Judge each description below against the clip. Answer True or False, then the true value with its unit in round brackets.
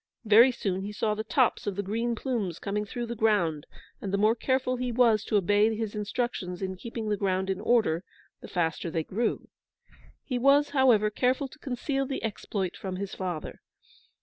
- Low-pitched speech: False (215 Hz)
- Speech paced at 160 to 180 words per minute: False (190 wpm)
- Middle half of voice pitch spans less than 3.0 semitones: False (3.9 semitones)